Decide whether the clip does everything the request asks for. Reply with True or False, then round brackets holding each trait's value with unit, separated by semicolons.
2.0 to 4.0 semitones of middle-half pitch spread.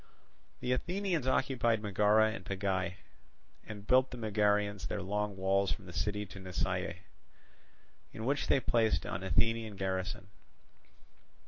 True (3.1 semitones)